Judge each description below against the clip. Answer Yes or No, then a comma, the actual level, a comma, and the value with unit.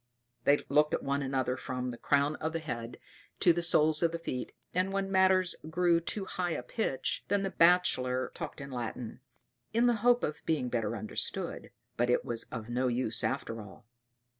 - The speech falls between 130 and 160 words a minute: No, average, 190 wpm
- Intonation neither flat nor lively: No, wide, 6.0 semitones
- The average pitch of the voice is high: No, medium, 150 Hz